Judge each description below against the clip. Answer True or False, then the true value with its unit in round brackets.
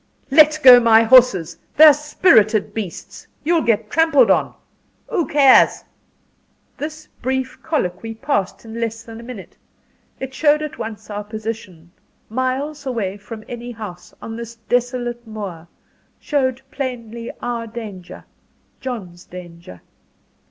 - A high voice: True (235 Hz)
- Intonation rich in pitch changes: False (3.7 semitones)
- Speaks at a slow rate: True (125 wpm)